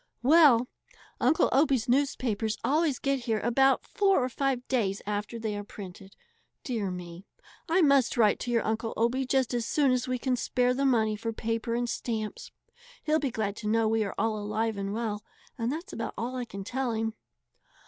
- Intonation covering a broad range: No, average, 3.4 semitones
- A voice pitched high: Yes, high, 235 Hz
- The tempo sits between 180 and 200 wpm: Yes, average, 190 wpm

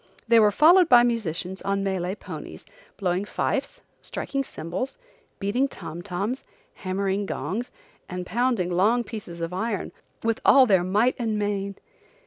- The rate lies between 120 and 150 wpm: Yes, average, 140 wpm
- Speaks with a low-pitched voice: No, high, 205 Hz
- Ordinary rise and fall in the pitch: Yes, average, 4.2 semitones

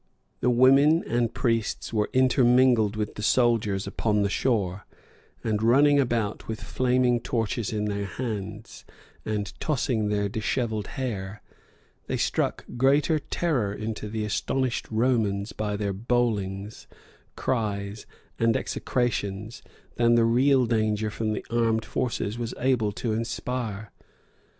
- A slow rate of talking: Yes, slow, 125 wpm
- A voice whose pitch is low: Yes, low, 115 Hz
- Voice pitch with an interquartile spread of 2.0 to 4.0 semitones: Yes, average, 2.8 semitones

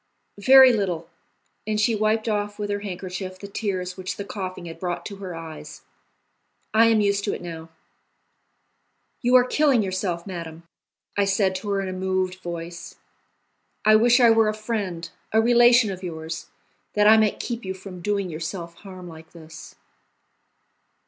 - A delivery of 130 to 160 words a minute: No, average, 170 wpm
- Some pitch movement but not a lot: Yes, average, 3.4 semitones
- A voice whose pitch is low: No, high, 195 Hz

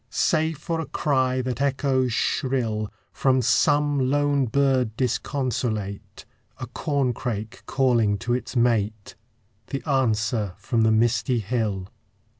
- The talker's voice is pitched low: Yes, low, 125 Hz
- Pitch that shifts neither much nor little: Yes, average, 3.7 semitones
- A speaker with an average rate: No, slow, 115 wpm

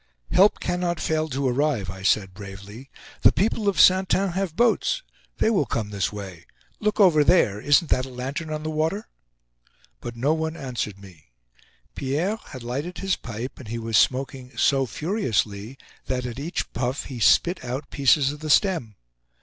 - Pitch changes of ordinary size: No, wide, 6.5 semitones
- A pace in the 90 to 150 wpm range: No, average, 175 wpm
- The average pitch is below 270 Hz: Yes, low, 135 Hz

